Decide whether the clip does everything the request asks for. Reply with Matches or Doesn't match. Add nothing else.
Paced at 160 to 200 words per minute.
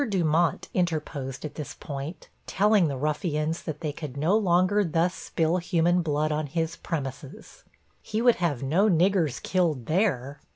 Doesn't match